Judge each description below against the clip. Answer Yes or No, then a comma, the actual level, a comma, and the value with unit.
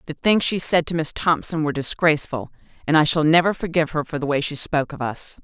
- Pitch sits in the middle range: Yes, medium, 155 Hz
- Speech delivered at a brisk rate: Yes, fast, 245 wpm